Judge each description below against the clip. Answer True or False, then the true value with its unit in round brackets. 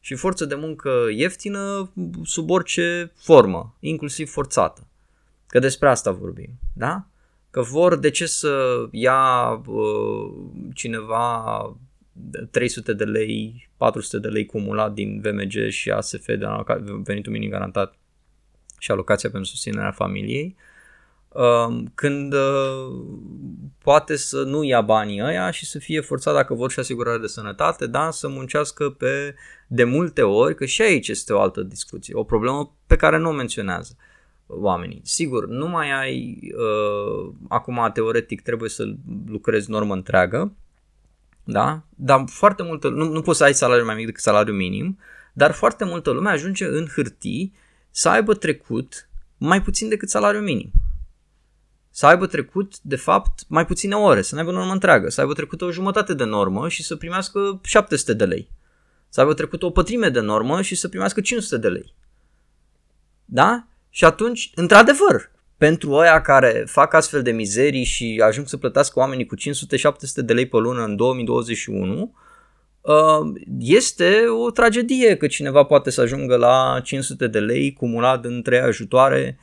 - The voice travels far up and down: True (6.8 semitones)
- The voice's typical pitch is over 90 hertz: True (140 Hz)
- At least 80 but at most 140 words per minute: False (155 wpm)